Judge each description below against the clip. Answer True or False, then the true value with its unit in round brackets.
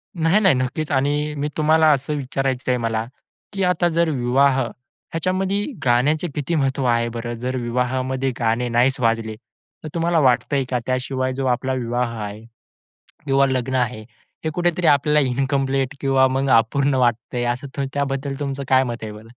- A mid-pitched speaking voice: False (130 Hz)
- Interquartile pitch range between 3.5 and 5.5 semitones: False (3.0 semitones)